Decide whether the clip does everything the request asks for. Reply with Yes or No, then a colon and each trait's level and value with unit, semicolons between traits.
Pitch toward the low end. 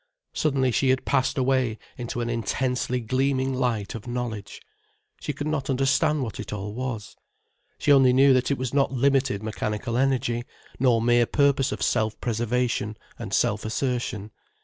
Yes: low, 125 Hz